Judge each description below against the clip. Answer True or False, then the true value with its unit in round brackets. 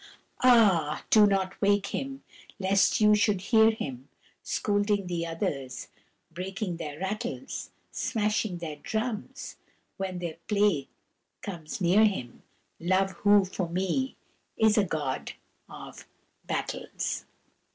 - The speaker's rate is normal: False (115 wpm)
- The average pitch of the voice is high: True (195 Hz)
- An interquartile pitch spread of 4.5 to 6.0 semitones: False (3.7 semitones)